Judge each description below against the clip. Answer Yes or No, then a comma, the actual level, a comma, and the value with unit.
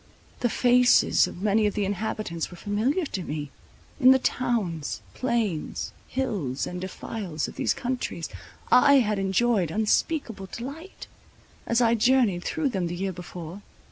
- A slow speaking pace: No, average, 145 wpm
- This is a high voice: Yes, high, 210 Hz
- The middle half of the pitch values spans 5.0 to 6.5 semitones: Yes, wide, 5.6 semitones